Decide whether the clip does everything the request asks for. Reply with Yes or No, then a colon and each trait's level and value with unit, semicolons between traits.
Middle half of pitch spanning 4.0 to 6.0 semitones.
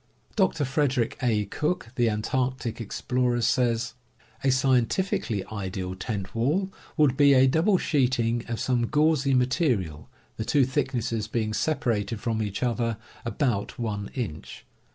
No: average, 3.5 semitones